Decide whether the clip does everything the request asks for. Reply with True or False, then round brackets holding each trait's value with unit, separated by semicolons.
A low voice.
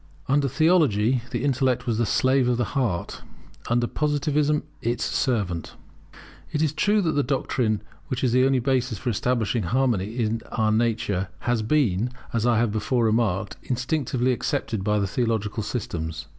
True (120 Hz)